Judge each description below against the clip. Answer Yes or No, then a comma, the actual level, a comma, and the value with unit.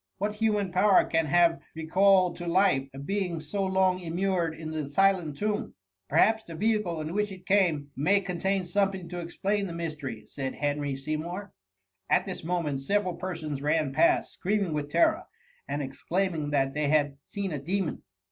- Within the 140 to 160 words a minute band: No, average, 175 wpm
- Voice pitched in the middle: Yes, medium, 175 Hz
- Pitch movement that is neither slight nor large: Yes, average, 4.5 semitones